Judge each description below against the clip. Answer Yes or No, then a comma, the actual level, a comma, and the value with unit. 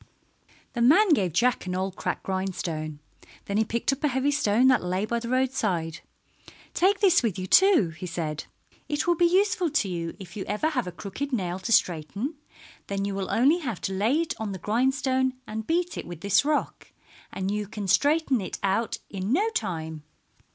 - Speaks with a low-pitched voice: No, high, 215 Hz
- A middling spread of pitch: No, wide, 7.1 semitones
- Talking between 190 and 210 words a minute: Yes, average, 200 wpm